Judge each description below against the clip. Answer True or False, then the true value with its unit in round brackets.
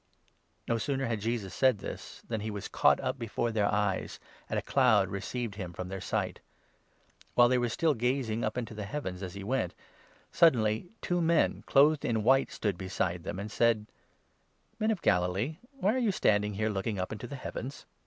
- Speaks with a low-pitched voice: True (110 Hz)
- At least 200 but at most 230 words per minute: True (205 wpm)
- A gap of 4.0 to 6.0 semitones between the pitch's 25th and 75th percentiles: True (4.9 semitones)